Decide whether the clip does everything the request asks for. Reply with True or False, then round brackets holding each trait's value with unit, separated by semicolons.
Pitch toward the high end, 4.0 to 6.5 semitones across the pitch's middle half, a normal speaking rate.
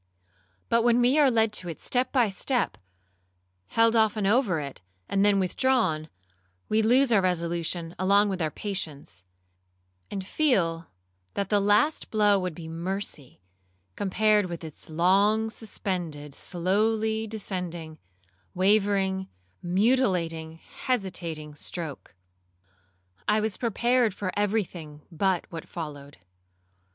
False (195 Hz; 4.6 semitones; 120 wpm)